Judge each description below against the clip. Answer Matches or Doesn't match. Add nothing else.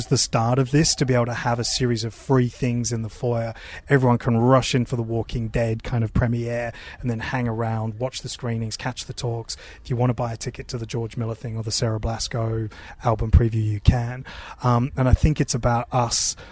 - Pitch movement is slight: Matches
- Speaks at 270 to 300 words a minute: Doesn't match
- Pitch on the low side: Matches